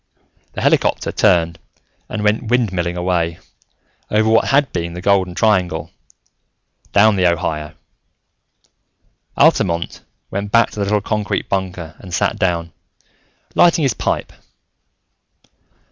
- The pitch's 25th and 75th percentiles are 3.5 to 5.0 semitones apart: Yes, average, 3.8 semitones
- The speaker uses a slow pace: Yes, slow, 115 wpm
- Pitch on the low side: Yes, very low, 95 Hz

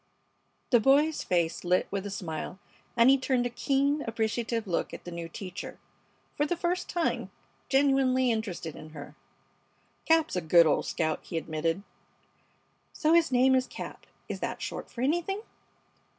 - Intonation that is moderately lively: No, wide, 8.1 semitones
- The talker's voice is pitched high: Yes, high, 235 Hz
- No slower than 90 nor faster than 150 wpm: No, average, 160 wpm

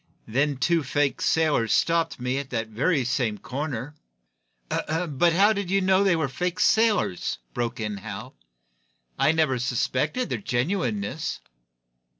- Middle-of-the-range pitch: Yes, medium, 145 Hz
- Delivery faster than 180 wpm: No, average, 140 wpm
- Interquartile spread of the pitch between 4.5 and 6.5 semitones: Yes, wide, 5.6 semitones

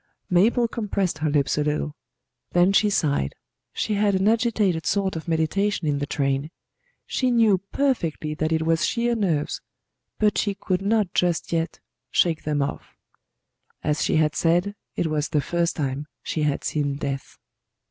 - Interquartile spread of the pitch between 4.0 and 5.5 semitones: Yes, average, 5.1 semitones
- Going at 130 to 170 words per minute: Yes, average, 165 wpm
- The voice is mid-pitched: Yes, medium, 170 Hz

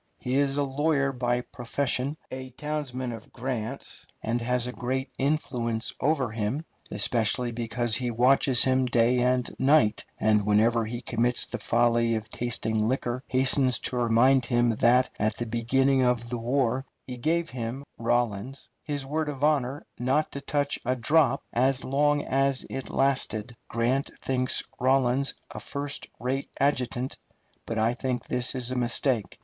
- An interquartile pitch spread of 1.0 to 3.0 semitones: Yes, narrow, 2.5 semitones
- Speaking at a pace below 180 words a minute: Yes, average, 155 wpm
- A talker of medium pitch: No, low, 125 Hz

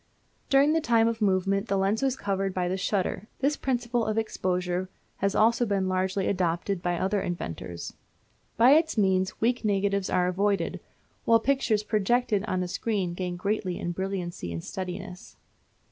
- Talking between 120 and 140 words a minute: No, average, 165 wpm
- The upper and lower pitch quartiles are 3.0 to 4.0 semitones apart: Yes, average, 3.5 semitones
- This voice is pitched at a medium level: No, high, 195 Hz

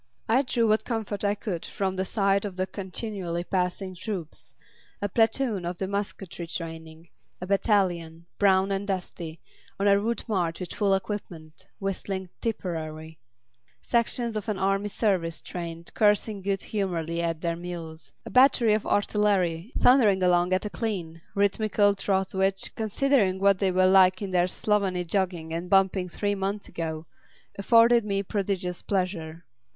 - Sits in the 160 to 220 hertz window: Yes, high, 190 Hz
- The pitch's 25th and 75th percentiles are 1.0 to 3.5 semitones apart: Yes, average, 2.8 semitones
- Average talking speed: Yes, average, 155 wpm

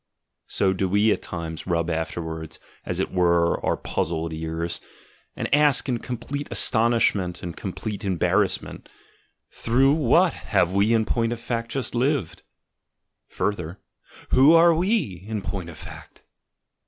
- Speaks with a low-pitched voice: Yes, low, 100 Hz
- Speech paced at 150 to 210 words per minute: No, average, 140 wpm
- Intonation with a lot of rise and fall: Yes, wide, 6.2 semitones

